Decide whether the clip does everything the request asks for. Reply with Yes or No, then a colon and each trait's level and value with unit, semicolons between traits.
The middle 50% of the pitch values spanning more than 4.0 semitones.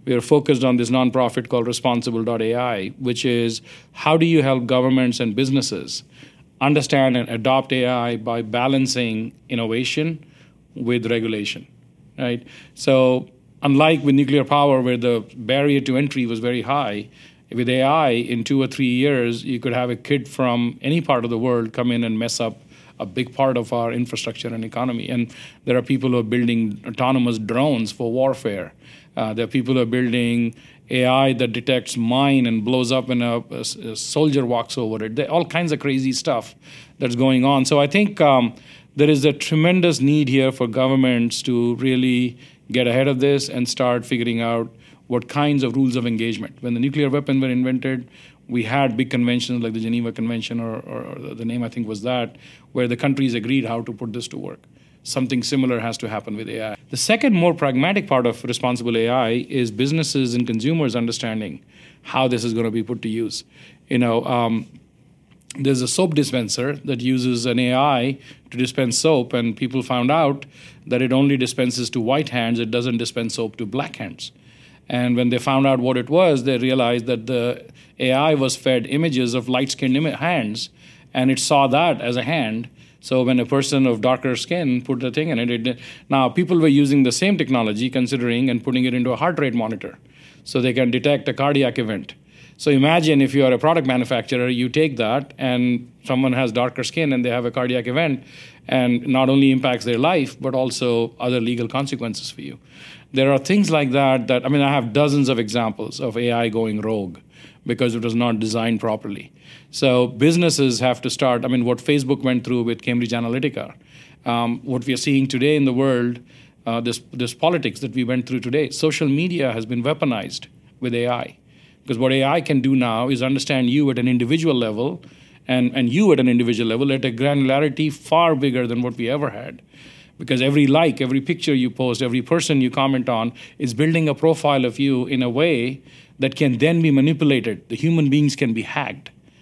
No: narrow, 2.4 semitones